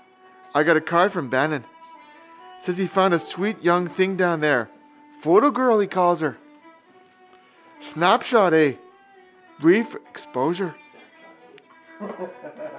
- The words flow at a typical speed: No, slow, 115 wpm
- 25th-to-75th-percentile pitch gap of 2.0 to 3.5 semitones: No, average, 4.2 semitones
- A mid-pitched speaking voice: Yes, medium, 180 Hz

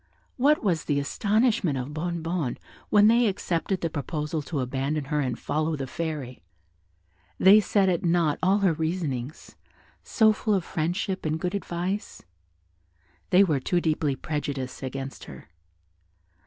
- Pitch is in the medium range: Yes, medium, 165 Hz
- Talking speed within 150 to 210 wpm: No, average, 140 wpm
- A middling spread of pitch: Yes, average, 4.7 semitones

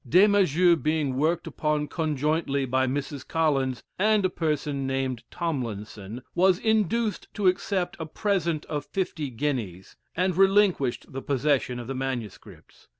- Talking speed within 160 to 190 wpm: No, average, 140 wpm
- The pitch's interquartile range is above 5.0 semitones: Yes, wide, 5.4 semitones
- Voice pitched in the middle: Yes, medium, 150 Hz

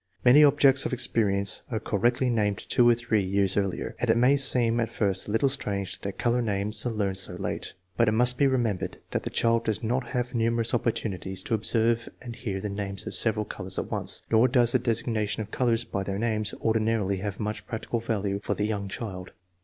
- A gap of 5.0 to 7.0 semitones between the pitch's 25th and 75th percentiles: No, average, 3.0 semitones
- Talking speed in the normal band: No, fast, 215 wpm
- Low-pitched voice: Yes, low, 110 Hz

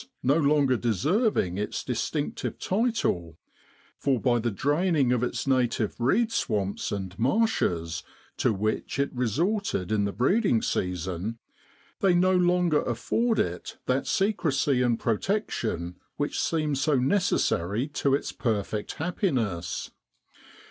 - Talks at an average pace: No, slow, 120 wpm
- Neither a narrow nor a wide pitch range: No, wide, 8.8 semitones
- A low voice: Yes, low, 130 Hz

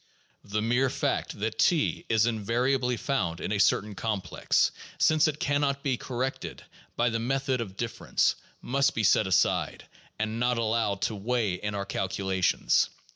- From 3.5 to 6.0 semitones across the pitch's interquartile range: Yes, average, 4.2 semitones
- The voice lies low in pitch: Yes, low, 115 Hz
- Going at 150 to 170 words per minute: Yes, average, 160 wpm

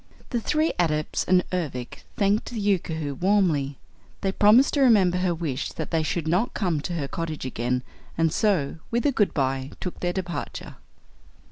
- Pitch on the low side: No, medium, 175 Hz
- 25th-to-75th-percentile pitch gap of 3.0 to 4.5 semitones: No, average, 4.9 semitones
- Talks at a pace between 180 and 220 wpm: No, average, 170 wpm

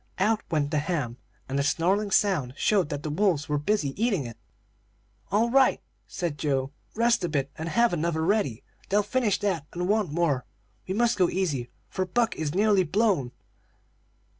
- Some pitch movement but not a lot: No, wide, 6.1 semitones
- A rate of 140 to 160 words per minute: No, average, 180 wpm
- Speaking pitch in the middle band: Yes, medium, 175 Hz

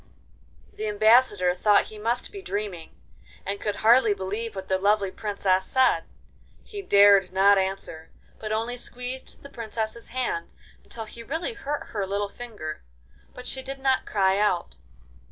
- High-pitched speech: Yes, high, 215 Hz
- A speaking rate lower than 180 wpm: Yes, average, 155 wpm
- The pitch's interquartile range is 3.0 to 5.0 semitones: Yes, average, 4.0 semitones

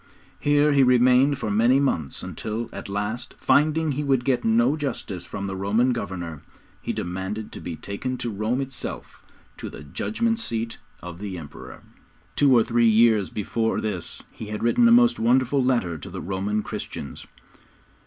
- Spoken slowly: No, average, 170 wpm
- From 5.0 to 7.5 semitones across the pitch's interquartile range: Yes, average, 5.3 semitones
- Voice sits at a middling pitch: No, low, 115 Hz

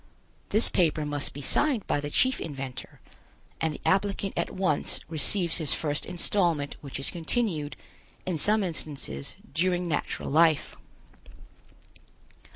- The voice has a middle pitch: Yes, medium, 160 Hz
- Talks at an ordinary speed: No, slow, 130 wpm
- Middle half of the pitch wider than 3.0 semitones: Yes, average, 4.4 semitones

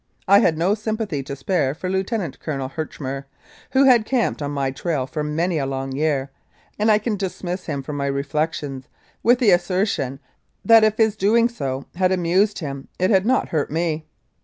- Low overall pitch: No, medium, 170 Hz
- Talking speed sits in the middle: Yes, average, 190 wpm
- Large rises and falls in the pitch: Yes, wide, 6.8 semitones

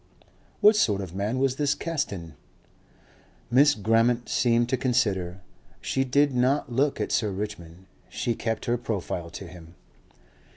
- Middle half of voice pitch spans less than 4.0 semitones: No, average, 5.2 semitones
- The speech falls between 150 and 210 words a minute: No, average, 140 wpm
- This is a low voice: Yes, low, 115 Hz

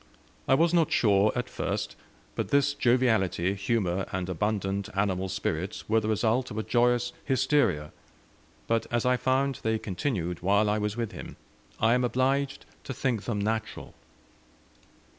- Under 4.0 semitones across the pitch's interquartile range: No, average, 4.3 semitones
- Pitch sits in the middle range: No, low, 110 Hz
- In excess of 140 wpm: Yes, average, 155 wpm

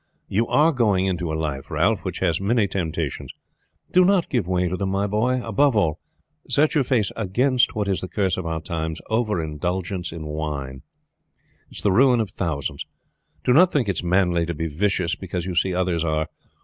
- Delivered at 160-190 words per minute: No, average, 200 wpm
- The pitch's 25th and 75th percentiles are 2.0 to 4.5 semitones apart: No, average, 5.0 semitones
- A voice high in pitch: No, very low, 95 Hz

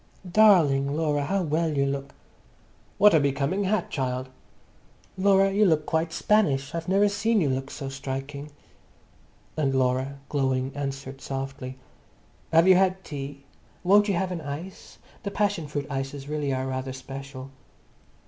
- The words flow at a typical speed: Yes, average, 150 wpm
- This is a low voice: No, medium, 145 Hz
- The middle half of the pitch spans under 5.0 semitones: No, average, 5.3 semitones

